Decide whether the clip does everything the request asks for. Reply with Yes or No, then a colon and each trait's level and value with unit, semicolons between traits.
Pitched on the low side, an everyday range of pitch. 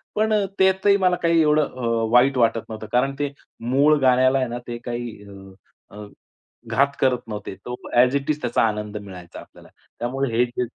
Yes: low, 125 Hz; average, 3.2 semitones